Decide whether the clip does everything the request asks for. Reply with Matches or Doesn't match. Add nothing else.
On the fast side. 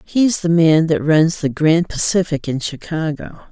Doesn't match